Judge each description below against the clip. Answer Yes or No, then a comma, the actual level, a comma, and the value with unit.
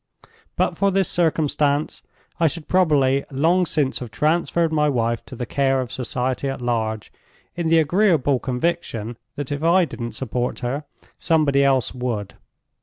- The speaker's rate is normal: Yes, average, 150 wpm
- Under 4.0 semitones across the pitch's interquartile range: No, average, 4.7 semitones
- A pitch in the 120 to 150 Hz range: Yes, medium, 140 Hz